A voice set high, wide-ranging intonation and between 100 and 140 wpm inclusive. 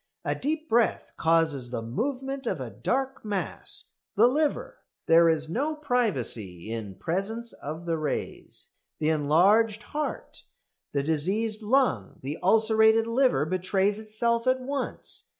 Yes: high, 210 Hz; wide, 7.7 semitones; slow, 135 wpm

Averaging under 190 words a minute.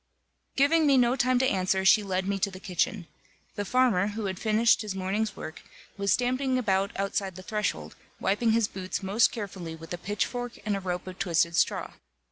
No: average, 195 wpm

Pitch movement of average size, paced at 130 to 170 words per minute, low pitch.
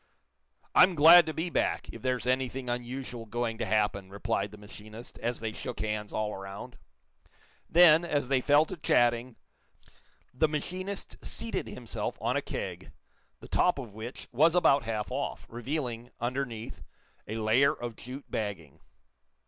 Yes: average, 4.9 semitones; average, 150 wpm; low, 120 Hz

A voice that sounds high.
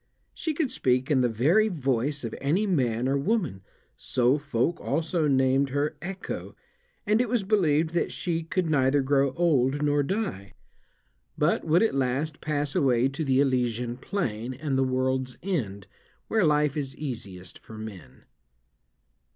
No: medium, 140 Hz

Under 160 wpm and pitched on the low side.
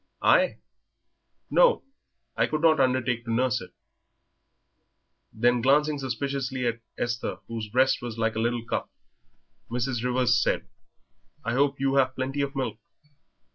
Yes: slow, 135 wpm; low, 130 Hz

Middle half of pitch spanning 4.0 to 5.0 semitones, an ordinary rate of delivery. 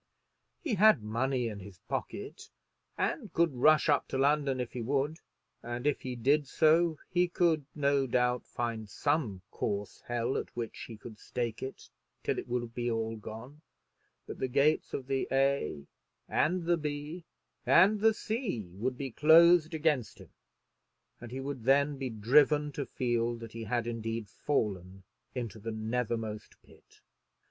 Yes: average, 4.5 semitones; average, 160 wpm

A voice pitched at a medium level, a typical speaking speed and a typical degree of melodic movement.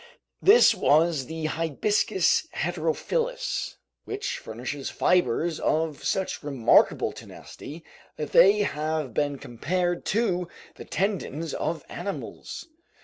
No: medium, 165 Hz; slow, 100 wpm; average, 4.5 semitones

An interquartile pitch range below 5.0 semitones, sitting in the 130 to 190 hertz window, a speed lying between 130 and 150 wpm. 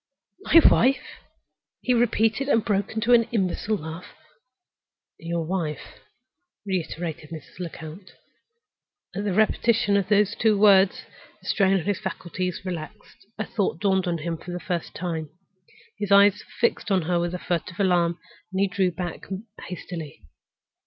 Yes: average, 3.2 semitones; medium, 185 Hz; average, 145 wpm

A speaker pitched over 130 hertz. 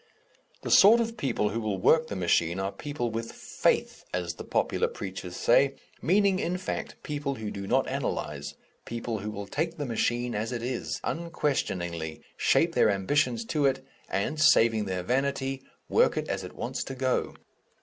No: low, 120 Hz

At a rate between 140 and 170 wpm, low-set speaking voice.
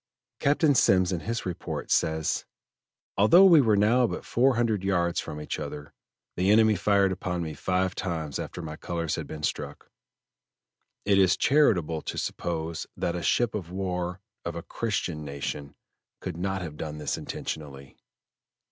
Yes: average, 160 wpm; very low, 90 Hz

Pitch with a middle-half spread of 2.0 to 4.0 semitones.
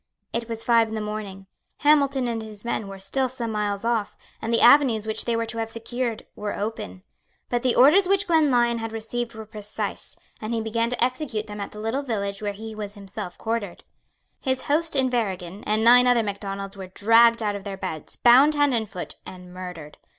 Yes: average, 3.0 semitones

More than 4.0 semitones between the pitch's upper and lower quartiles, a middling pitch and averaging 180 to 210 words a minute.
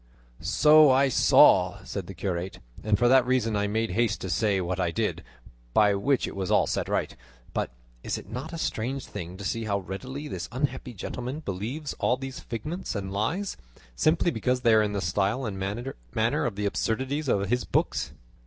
No: average, 4.9 semitones; low, 110 Hz; average, 195 wpm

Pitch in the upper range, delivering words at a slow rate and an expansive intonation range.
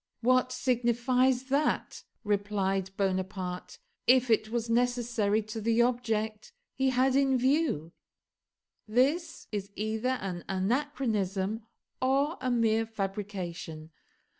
No: high, 225 Hz; slow, 105 wpm; average, 4.1 semitones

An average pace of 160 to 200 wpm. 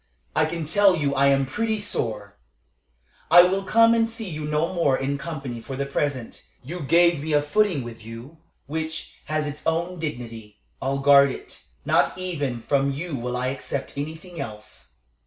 Yes: average, 175 wpm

